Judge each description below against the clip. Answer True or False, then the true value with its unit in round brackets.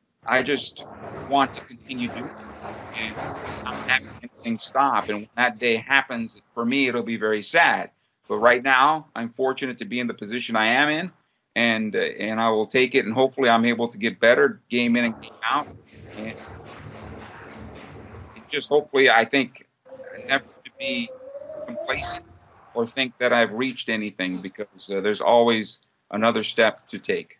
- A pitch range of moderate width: True (3.4 semitones)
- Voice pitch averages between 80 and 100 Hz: False (120 Hz)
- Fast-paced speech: False (170 wpm)